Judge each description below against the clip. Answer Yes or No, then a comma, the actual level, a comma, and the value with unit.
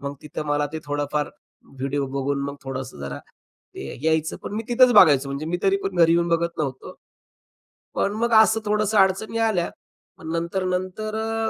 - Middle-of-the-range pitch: Yes, medium, 165 Hz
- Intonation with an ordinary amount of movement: No, wide, 5.7 semitones